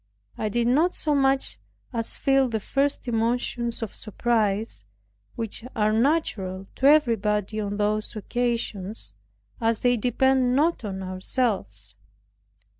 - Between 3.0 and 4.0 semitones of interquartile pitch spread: Yes, average, 3.6 semitones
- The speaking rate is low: Yes, slow, 120 wpm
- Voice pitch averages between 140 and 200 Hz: No, high, 230 Hz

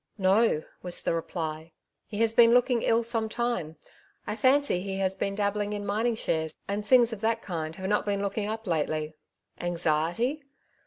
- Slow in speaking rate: No, average, 180 wpm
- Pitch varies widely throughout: No, average, 4.8 semitones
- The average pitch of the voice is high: Yes, high, 205 Hz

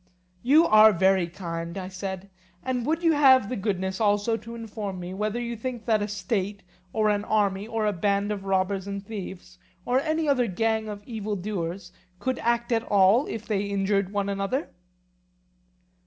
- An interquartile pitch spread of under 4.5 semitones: Yes, average, 3.0 semitones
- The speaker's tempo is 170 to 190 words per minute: Yes, average, 180 wpm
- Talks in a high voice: Yes, high, 205 Hz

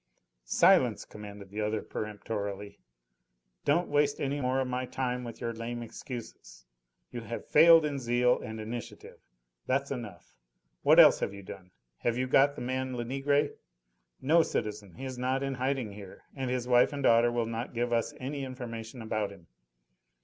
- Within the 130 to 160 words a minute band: No, average, 170 wpm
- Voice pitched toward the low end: Yes, low, 120 Hz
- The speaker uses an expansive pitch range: No, average, 3.5 semitones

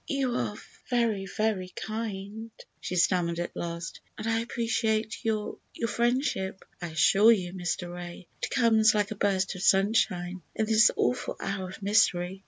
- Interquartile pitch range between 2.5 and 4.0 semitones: Yes, average, 3.4 semitones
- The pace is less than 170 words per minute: Yes, average, 155 wpm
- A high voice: Yes, high, 205 Hz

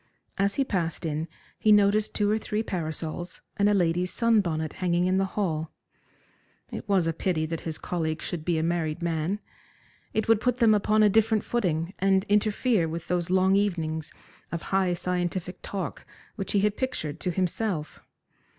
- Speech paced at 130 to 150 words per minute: No, average, 180 wpm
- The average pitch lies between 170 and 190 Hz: Yes, medium, 185 Hz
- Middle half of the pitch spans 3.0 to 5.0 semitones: Yes, average, 3.9 semitones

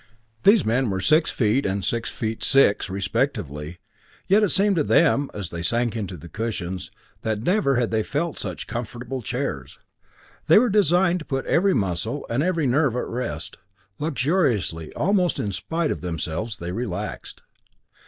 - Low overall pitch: Yes, low, 120 Hz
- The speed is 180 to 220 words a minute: No, average, 165 wpm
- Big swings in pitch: Yes, wide, 8.3 semitones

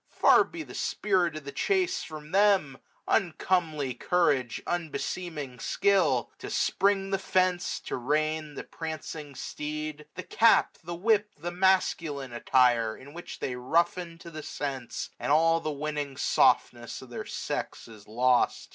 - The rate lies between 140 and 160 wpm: Yes, average, 155 wpm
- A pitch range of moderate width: Yes, average, 4.7 semitones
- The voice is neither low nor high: Yes, medium, 155 Hz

